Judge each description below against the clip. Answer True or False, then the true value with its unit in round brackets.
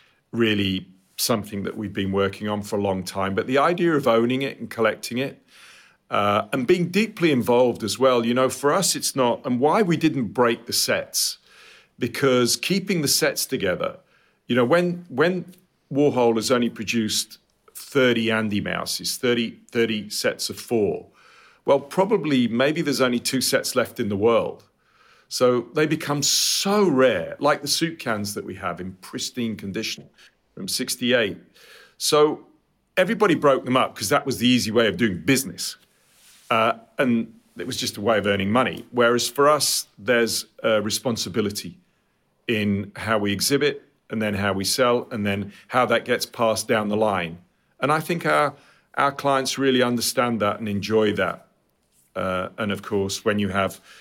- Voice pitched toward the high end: False (120 Hz)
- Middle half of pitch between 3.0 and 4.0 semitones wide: False (5.0 semitones)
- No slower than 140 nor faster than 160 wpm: False (175 wpm)